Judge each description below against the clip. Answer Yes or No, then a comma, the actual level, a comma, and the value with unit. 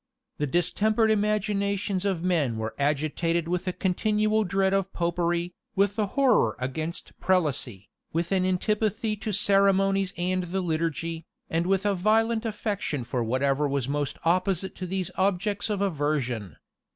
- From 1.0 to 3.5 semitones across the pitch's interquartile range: No, average, 4.2 semitones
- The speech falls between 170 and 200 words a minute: No, average, 145 wpm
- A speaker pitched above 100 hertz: Yes, medium, 185 Hz